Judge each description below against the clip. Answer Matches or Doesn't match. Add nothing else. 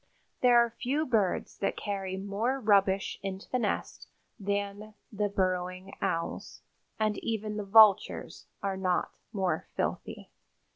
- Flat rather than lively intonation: Matches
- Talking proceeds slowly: Matches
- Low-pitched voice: Doesn't match